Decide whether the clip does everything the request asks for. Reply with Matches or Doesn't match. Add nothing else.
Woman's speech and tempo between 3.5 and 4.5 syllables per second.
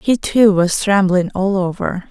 Matches